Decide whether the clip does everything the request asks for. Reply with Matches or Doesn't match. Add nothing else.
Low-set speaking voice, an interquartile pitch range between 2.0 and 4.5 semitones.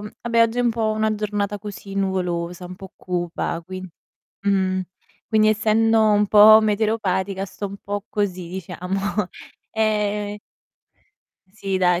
Doesn't match